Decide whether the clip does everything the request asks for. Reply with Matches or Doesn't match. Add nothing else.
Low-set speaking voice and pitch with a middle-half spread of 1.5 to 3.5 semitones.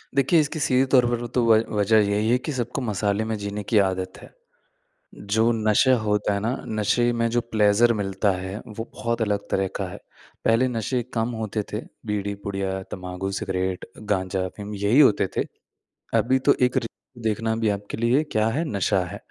Matches